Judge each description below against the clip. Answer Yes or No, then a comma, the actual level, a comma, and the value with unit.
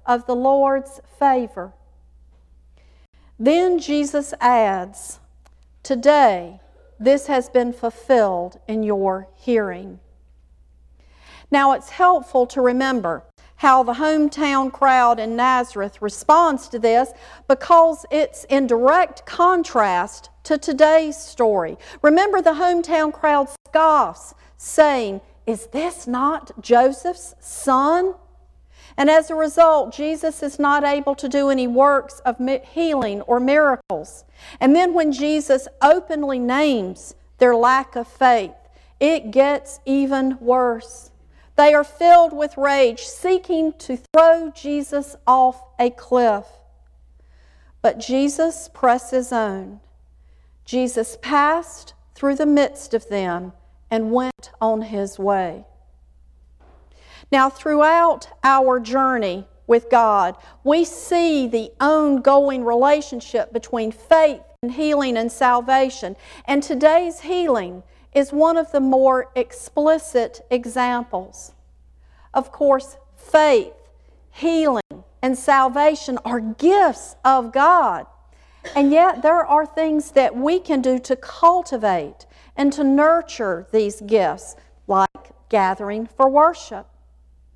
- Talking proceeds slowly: Yes, slow, 110 wpm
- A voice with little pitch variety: No, average, 5.1 semitones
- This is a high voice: Yes, very high, 265 Hz